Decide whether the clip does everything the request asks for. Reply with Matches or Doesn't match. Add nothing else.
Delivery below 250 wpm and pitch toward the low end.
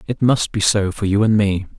Doesn't match